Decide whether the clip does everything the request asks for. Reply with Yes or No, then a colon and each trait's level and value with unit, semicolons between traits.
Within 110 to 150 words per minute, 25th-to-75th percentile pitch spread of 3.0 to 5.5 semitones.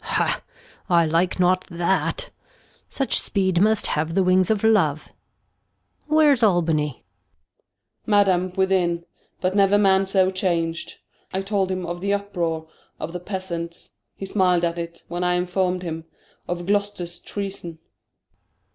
No: average, 145 wpm; narrow, 2.4 semitones